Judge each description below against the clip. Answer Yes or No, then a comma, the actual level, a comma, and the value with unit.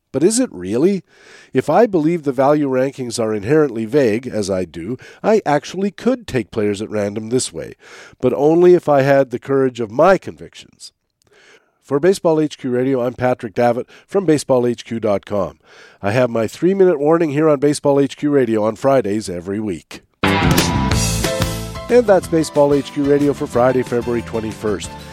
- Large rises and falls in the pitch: No, average, 4.9 semitones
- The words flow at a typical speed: Yes, average, 160 wpm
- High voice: No, low, 130 Hz